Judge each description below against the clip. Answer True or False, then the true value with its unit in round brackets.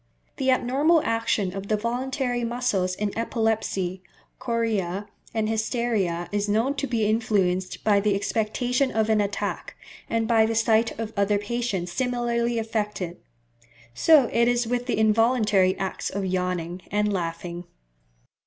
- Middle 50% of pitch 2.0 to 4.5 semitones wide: True (3.3 semitones)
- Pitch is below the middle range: False (220 Hz)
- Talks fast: False (140 wpm)